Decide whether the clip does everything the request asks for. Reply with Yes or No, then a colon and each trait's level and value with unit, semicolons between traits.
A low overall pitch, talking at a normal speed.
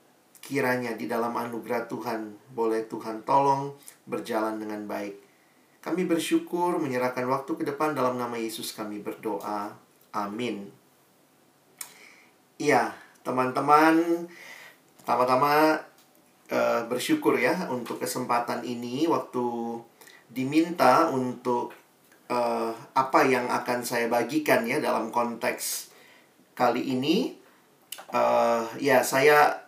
Yes: low, 125 Hz; average, 100 wpm